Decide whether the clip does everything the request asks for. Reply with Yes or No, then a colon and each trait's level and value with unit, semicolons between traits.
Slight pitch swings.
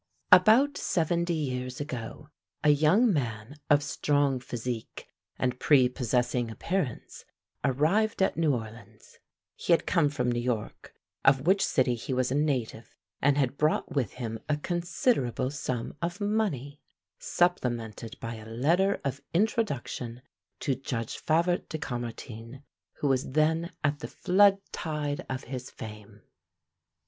No: average, 5.2 semitones